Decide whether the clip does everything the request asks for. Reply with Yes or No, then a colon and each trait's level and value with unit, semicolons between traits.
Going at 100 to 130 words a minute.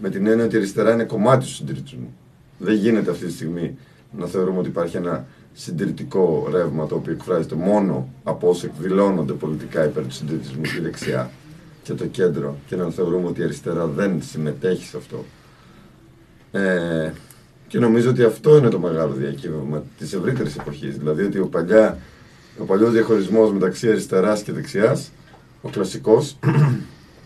No: average, 155 wpm